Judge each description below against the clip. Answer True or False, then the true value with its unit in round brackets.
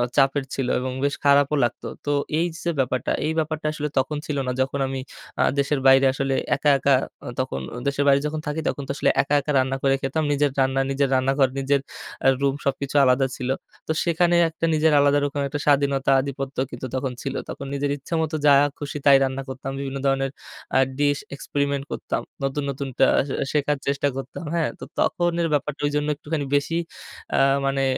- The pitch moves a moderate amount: False (1.5 semitones)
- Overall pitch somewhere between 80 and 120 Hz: False (140 Hz)